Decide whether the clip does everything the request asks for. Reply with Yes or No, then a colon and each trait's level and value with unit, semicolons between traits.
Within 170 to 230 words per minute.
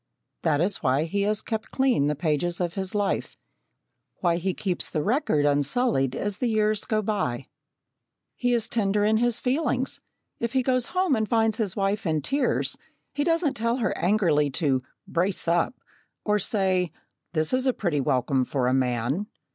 Yes: average, 175 wpm